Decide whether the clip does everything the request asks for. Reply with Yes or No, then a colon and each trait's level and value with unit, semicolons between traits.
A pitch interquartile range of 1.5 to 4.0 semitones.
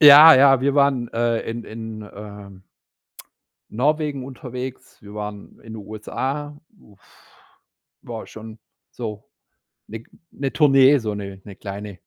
No: average, 4.5 semitones